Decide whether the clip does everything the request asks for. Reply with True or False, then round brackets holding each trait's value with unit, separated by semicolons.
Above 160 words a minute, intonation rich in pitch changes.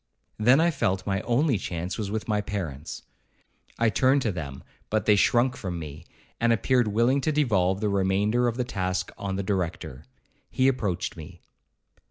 False (175 wpm; 4.7 semitones)